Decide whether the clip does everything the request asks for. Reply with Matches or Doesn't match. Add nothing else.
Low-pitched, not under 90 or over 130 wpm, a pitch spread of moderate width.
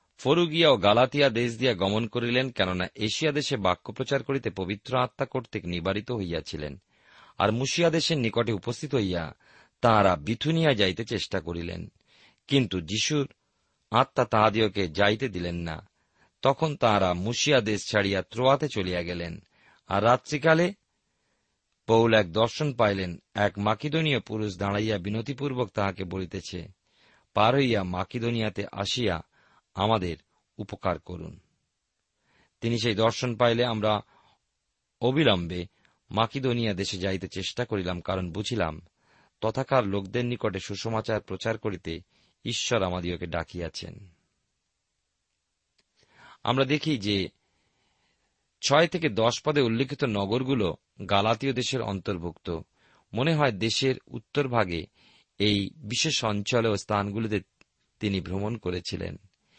Matches